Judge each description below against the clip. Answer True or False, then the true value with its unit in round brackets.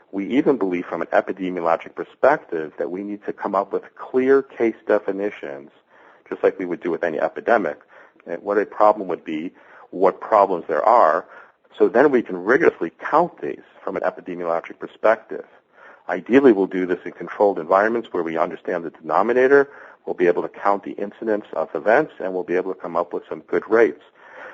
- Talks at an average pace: True (190 wpm)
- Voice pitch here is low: True (100 Hz)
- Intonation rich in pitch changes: True (5.9 semitones)